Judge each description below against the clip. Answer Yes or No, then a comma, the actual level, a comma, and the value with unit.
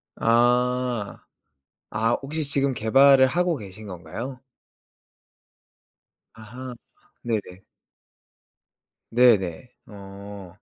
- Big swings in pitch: No, average, 4.2 semitones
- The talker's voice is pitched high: No, low, 120 Hz